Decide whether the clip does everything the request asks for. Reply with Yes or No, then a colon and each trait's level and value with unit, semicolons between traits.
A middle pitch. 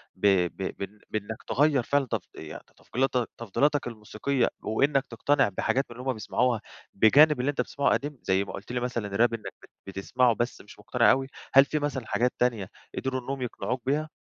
No: low, 125 Hz